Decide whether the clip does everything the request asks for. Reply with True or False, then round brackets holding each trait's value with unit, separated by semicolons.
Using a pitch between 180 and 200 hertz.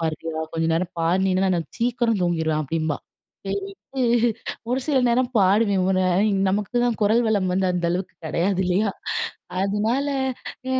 True (190 Hz)